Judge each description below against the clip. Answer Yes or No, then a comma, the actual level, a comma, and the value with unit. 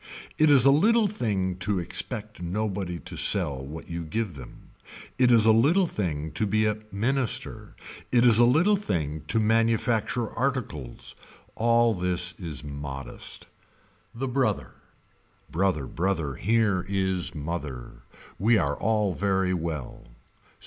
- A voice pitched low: Yes, low, 100 Hz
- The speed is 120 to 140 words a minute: Yes, slow, 135 wpm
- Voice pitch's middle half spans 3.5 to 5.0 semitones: No, wide, 5.6 semitones